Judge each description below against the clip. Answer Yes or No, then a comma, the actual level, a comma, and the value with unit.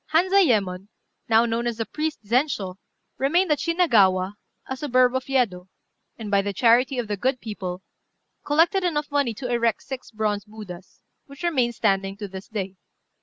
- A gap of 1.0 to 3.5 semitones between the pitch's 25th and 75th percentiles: No, wide, 5.6 semitones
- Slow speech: No, average, 160 wpm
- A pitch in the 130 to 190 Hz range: No, high, 235 Hz